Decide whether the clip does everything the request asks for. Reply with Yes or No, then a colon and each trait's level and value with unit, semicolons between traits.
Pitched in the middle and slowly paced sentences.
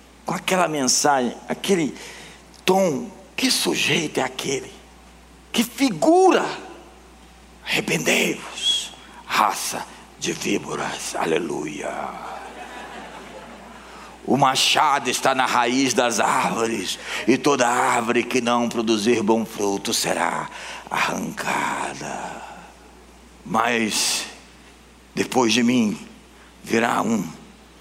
No: low, 125 Hz; slow, 80 wpm